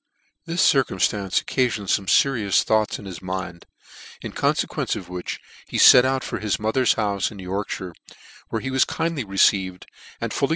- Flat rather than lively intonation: No, average, 5.3 semitones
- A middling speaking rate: Yes, average, 165 wpm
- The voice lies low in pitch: Yes, low, 105 Hz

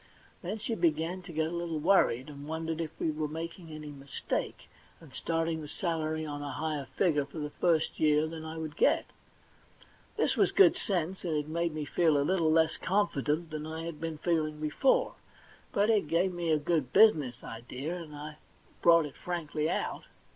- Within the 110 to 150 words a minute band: No, average, 190 wpm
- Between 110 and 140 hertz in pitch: No, medium, 160 Hz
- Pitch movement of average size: No, narrow, 2.1 semitones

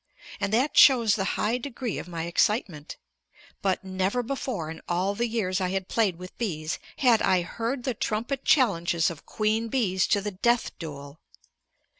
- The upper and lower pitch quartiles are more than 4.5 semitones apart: Yes, average, 4.9 semitones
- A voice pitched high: Yes, high, 200 Hz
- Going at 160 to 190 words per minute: Yes, average, 170 wpm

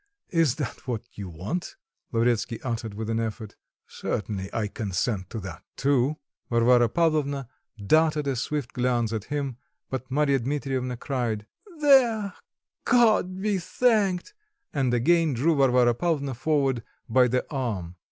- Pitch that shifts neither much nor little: Yes, average, 5.0 semitones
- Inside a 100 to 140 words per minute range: Yes, slow, 135 wpm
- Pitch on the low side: Yes, low, 130 Hz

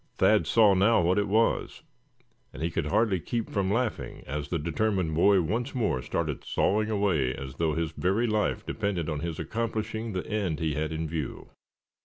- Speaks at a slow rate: No, average, 185 wpm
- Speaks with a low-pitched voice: Yes, very low, 95 Hz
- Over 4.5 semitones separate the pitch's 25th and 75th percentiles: Yes, average, 5.3 semitones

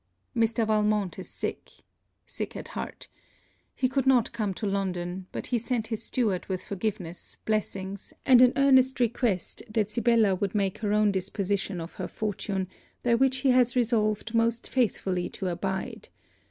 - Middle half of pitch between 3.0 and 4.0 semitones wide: Yes, average, 3.7 semitones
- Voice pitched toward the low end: No, high, 215 Hz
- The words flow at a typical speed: Yes, average, 160 wpm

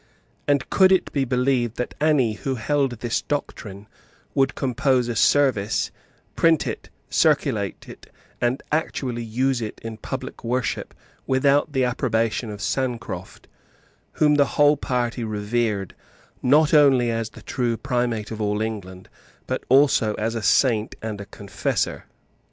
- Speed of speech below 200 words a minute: Yes, average, 140 wpm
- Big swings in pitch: No, average, 3.5 semitones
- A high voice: No, low, 120 Hz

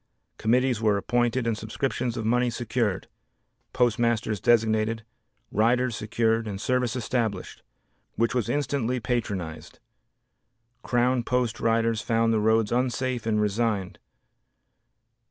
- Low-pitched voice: Yes, low, 115 Hz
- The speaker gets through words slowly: Yes, slow, 110 wpm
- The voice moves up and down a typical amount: No, narrow, 2.1 semitones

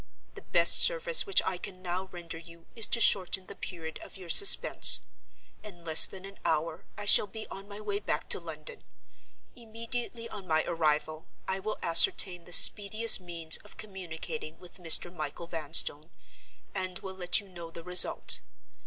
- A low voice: No, medium, 180 Hz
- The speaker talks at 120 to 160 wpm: No, average, 170 wpm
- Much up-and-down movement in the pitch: No, average, 3.8 semitones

